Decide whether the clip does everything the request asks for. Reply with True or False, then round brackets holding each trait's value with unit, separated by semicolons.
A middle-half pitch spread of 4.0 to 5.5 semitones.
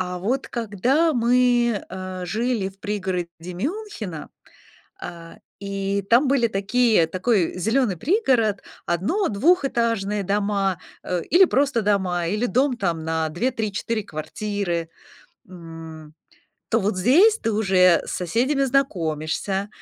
True (5.2 semitones)